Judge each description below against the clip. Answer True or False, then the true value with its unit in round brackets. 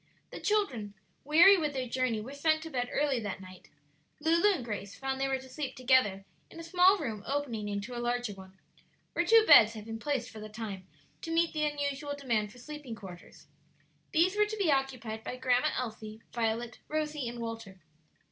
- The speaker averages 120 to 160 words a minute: False (195 wpm)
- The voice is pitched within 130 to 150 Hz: False (255 Hz)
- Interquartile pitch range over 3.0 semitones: True (5.3 semitones)